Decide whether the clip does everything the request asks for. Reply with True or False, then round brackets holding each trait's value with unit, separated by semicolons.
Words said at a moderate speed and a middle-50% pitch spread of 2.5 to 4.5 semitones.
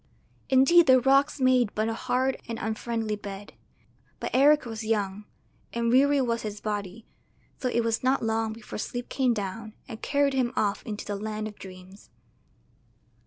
True (165 wpm; 3.4 semitones)